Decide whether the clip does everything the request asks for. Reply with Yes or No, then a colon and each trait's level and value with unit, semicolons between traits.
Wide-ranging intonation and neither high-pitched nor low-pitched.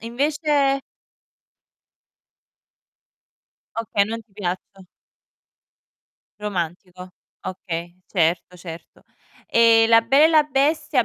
No: wide, 7.0 semitones; high, 225 Hz